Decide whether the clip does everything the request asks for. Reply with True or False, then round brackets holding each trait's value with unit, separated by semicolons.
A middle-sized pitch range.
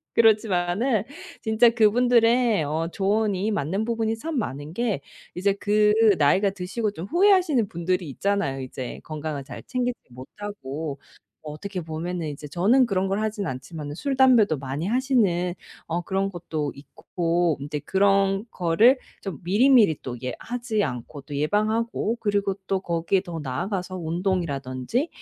False (5.7 semitones)